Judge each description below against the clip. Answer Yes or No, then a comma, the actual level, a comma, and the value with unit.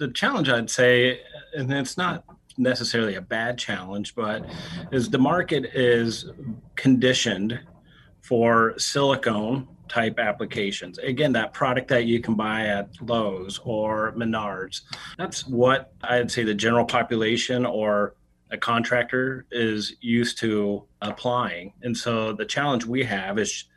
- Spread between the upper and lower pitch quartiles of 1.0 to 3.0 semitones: Yes, average, 2.7 semitones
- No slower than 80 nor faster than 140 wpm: Yes, slow, 135 wpm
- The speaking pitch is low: Yes, low, 120 Hz